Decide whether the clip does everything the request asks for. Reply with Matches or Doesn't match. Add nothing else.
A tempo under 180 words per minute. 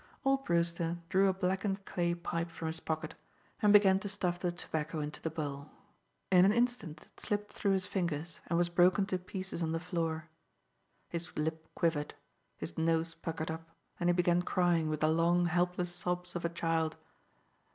Doesn't match